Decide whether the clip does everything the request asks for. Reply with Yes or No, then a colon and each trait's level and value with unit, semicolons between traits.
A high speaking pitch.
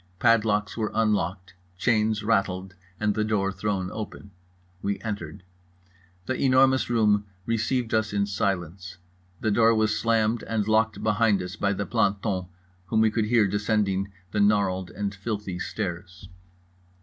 No: low, 105 Hz